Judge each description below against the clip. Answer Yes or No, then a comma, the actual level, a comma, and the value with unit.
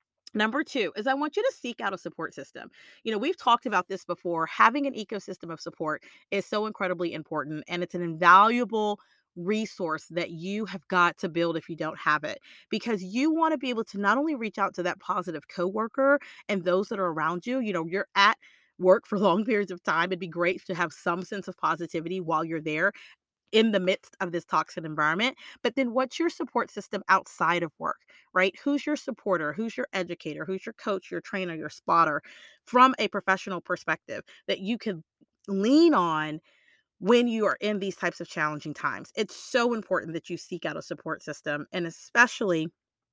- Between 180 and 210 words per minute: Yes, fast, 205 wpm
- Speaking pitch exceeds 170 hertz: Yes, high, 190 Hz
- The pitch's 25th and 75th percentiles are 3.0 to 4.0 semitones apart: No, average, 4.6 semitones